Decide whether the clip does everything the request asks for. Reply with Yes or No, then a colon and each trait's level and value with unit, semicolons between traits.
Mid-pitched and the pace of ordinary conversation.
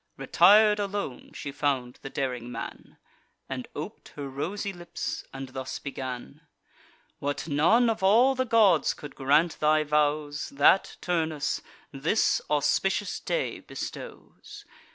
No: medium, 150 Hz; slow, 125 wpm